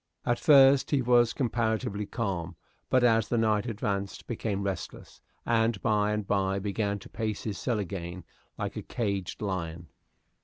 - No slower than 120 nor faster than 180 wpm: Yes, average, 155 wpm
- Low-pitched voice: Yes, low, 105 Hz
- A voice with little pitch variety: No, average, 3.0 semitones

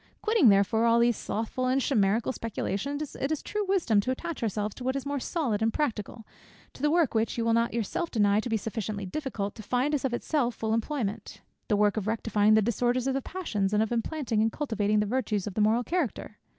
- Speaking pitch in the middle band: No, high, 230 Hz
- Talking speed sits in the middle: No, fast, 225 wpm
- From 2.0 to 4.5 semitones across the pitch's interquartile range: Yes, average, 4.2 semitones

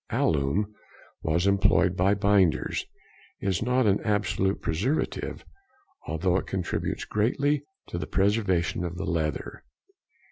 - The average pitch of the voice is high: No, very low, 95 Hz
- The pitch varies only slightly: No, average, 3.0 semitones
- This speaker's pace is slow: Yes, slow, 115 wpm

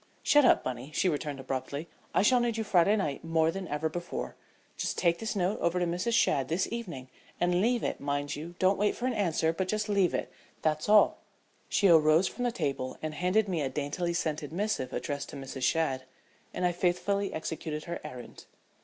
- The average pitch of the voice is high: No, medium, 170 Hz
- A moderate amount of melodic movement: Yes, average, 5.0 semitones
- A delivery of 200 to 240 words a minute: Yes, fast, 205 wpm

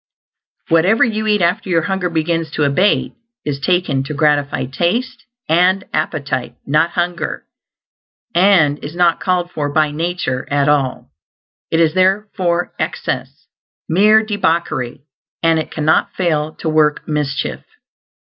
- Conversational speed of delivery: No, slow, 130 wpm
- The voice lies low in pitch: No, medium, 165 Hz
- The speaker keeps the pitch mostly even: No, average, 3.7 semitones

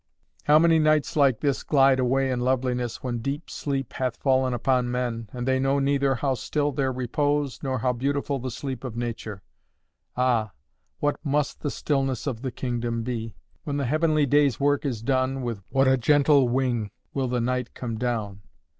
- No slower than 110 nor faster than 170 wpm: No, average, 185 wpm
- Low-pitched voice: Yes, low, 130 Hz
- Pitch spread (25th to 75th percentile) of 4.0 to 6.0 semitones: No, narrow, 2.5 semitones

